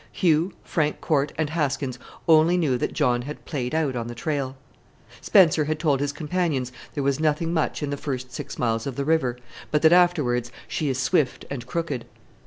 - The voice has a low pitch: No, medium, 145 Hz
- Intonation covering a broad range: No, average, 3.6 semitones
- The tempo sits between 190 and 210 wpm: Yes, average, 195 wpm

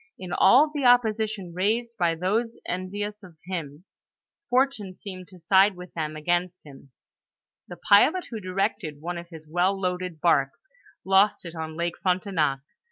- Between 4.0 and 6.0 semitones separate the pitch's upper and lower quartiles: No, average, 3.5 semitones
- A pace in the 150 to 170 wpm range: Yes, average, 155 wpm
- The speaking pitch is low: No, medium, 185 Hz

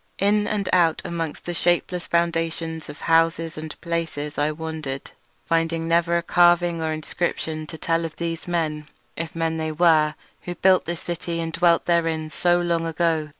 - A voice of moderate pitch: Yes, medium, 165 Hz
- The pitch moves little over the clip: Yes, narrow, 1.3 semitones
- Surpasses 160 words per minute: Yes, average, 170 wpm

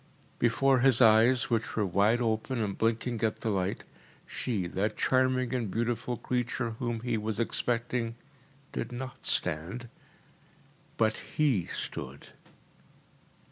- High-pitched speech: No, low, 115 Hz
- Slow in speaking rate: Yes, slow, 125 wpm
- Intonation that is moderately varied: No, narrow, 2.2 semitones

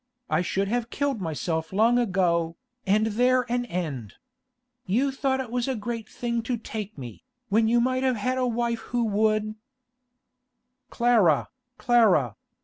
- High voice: Yes, high, 225 Hz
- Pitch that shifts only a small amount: No, average, 4.4 semitones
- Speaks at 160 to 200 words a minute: No, average, 150 wpm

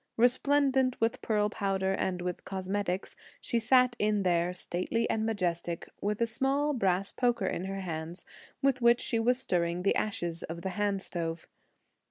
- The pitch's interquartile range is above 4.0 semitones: Yes, average, 4.7 semitones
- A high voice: Yes, high, 200 Hz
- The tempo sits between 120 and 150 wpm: No, average, 165 wpm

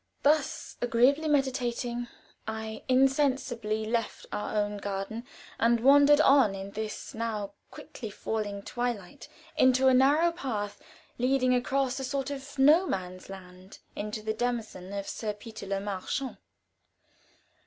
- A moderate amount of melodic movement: Yes, average, 4.4 semitones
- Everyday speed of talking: No, slow, 130 wpm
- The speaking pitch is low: No, high, 235 Hz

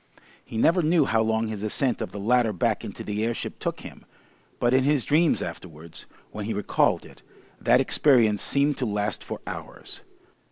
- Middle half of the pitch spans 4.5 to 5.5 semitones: Yes, average, 4.8 semitones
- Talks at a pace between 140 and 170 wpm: No, average, 185 wpm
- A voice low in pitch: Yes, low, 115 Hz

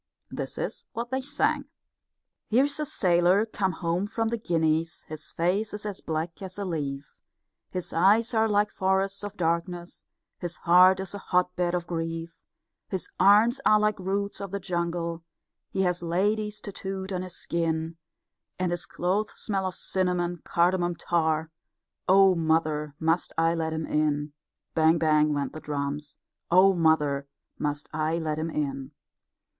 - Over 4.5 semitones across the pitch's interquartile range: No, average, 3.3 semitones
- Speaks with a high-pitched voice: No, medium, 175 Hz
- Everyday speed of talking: Yes, average, 155 wpm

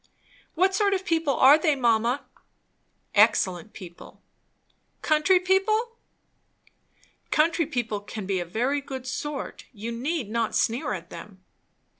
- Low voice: No, very high, 265 Hz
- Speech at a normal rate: No, slow, 130 wpm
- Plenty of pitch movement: Yes, wide, 7.3 semitones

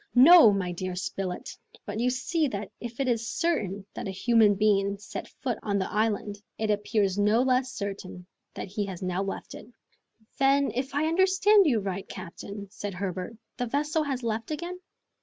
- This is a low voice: No, high, 215 Hz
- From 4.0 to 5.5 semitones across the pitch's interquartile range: Yes, average, 5.1 semitones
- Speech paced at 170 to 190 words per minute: Yes, average, 180 wpm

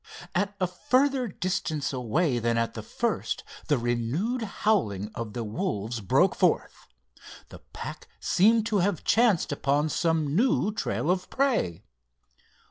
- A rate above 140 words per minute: No, slow, 135 wpm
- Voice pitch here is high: No, medium, 170 Hz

